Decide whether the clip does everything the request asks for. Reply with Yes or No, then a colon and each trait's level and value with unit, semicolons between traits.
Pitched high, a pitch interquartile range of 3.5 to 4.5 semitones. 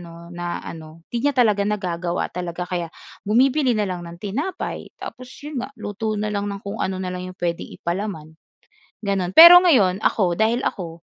Yes: high, 195 Hz; average, 3.9 semitones